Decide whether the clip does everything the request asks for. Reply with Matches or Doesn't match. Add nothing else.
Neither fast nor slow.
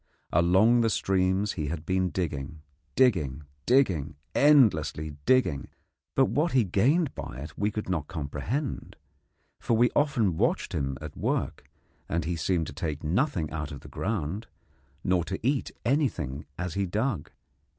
Matches